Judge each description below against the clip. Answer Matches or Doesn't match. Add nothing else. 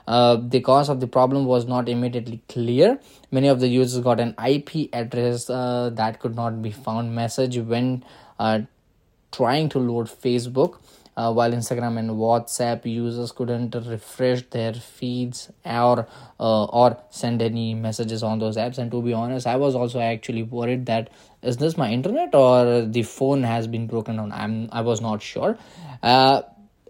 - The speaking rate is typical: Matches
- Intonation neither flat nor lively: Doesn't match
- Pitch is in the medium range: Doesn't match